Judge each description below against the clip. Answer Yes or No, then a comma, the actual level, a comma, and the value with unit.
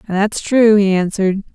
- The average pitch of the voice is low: No, high, 205 Hz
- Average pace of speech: Yes, average, 155 wpm